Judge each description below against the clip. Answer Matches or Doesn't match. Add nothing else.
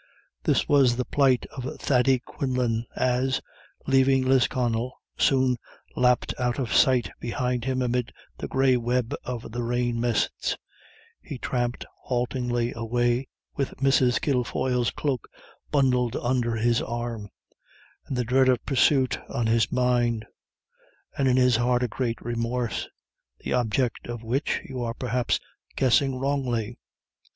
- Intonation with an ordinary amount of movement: Doesn't match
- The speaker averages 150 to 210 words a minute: Doesn't match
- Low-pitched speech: Matches